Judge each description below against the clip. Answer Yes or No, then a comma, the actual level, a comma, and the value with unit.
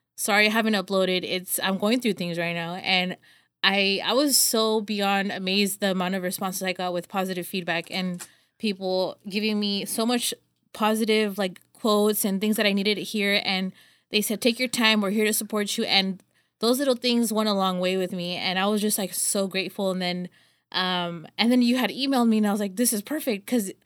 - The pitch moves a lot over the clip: No, average, 2.7 semitones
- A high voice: Yes, high, 200 Hz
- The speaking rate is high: Yes, fast, 220 wpm